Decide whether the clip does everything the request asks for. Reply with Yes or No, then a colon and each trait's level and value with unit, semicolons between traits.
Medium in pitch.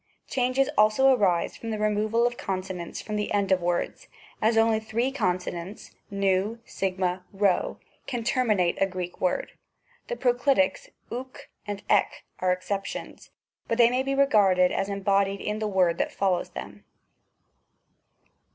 No: high, 205 Hz